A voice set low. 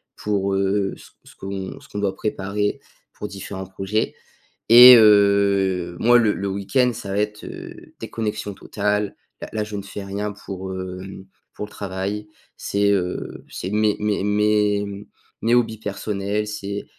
Yes: low, 100 Hz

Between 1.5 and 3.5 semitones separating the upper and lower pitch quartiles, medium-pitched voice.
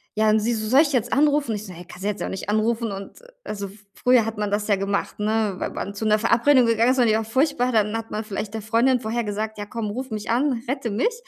No: narrow, 2.6 semitones; high, 220 Hz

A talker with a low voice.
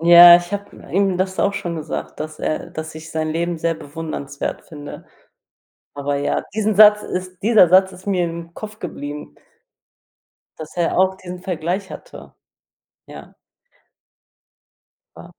No: medium, 175 Hz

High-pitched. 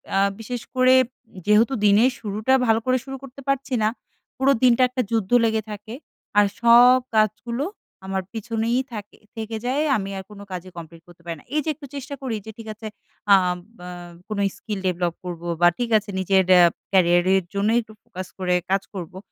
Yes: high, 215 Hz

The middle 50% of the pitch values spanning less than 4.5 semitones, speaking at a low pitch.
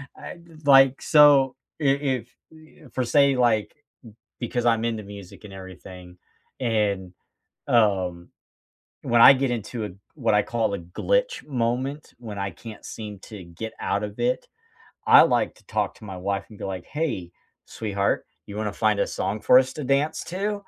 No: average, 5.2 semitones; low, 115 Hz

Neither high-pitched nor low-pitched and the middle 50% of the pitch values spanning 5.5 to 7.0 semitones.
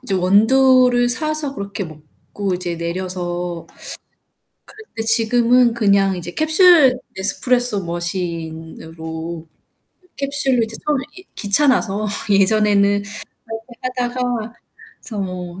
No: high, 205 Hz; wide, 5.9 semitones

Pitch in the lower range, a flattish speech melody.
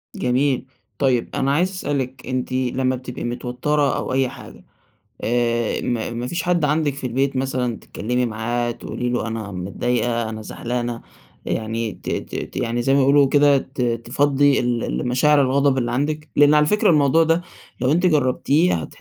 No: low, 130 Hz; average, 3.1 semitones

